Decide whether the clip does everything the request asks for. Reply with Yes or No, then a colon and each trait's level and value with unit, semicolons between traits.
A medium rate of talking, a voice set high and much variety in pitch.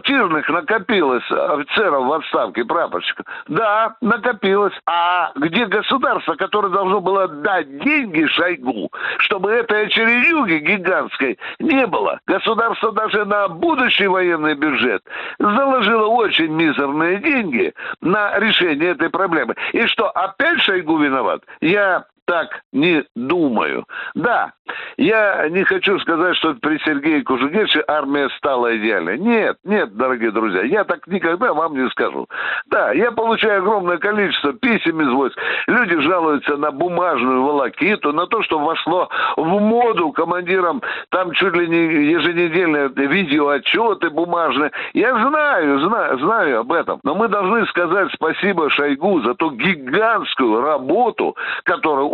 Yes: average, 130 wpm; high, 200 Hz; wide, 6.3 semitones